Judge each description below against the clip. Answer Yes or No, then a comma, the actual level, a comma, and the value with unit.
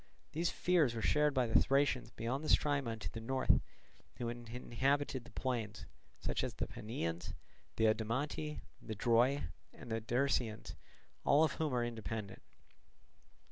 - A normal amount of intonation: Yes, average, 3.8 semitones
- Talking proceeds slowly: No, average, 145 wpm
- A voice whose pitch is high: No, low, 120 Hz